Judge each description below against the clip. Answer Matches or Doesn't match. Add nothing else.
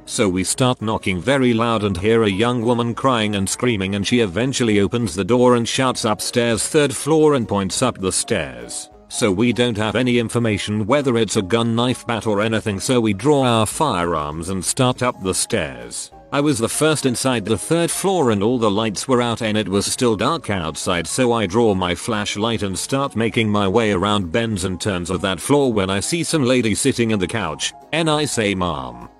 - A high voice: Doesn't match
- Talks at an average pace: Doesn't match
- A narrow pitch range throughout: Doesn't match